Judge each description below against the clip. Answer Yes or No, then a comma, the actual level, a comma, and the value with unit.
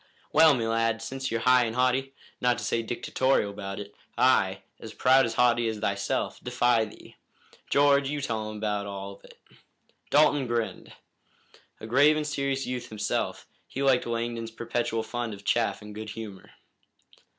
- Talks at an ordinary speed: Yes, average, 165 wpm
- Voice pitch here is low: Yes, low, 120 Hz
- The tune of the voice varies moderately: Yes, average, 3.2 semitones